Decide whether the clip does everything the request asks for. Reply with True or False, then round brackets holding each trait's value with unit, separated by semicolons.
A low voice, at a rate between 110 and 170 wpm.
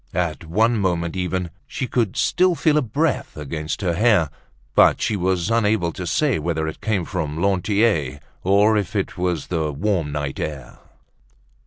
True (90 Hz; 165 wpm)